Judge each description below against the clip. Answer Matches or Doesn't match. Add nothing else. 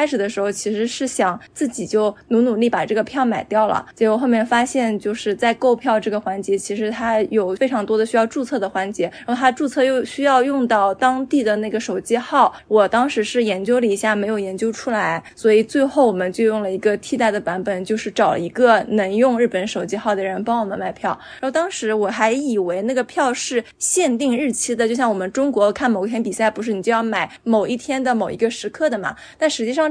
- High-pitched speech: Matches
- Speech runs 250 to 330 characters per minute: Doesn't match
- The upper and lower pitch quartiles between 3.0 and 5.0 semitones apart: Matches